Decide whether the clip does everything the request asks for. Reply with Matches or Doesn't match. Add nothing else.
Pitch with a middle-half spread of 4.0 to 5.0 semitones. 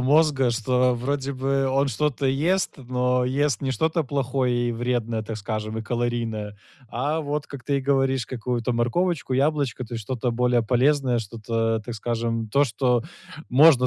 Doesn't match